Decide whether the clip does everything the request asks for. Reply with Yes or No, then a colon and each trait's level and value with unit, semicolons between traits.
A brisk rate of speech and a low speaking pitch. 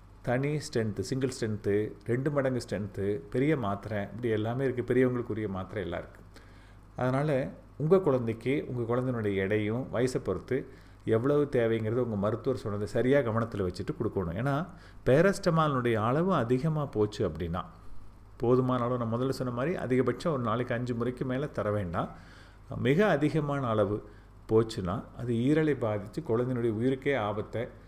Yes: fast, 135 wpm; low, 120 Hz